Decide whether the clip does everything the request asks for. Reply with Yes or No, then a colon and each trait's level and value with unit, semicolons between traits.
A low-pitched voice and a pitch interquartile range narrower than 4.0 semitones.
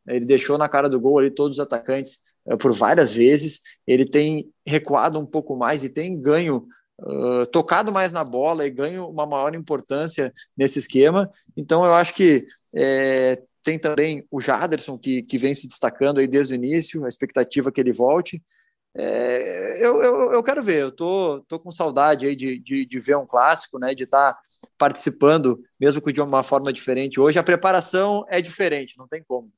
No: medium, 145 Hz; average, 3.5 semitones